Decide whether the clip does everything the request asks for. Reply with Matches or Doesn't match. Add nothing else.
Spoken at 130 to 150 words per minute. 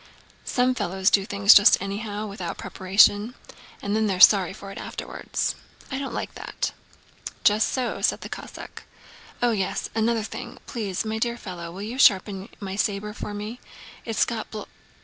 Doesn't match